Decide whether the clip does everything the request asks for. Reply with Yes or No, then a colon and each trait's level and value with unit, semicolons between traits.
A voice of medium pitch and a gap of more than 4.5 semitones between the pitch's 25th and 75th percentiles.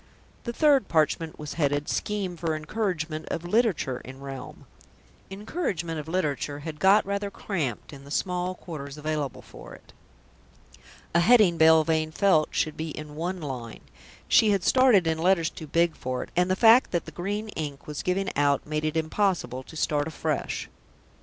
No: medium, 160 Hz; average, 4.2 semitones